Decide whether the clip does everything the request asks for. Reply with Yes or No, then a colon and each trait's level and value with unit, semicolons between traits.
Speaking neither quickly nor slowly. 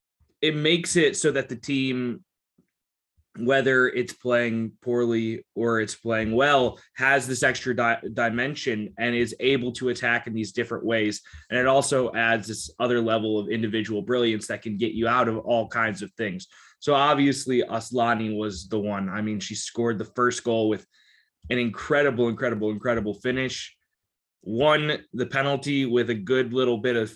Yes: average, 170 wpm